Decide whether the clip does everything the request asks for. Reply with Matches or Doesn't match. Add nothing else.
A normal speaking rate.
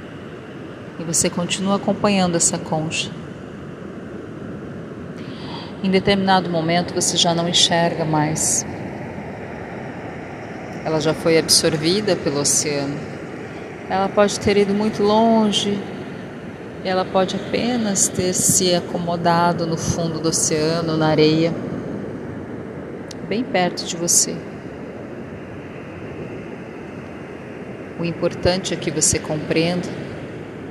Doesn't match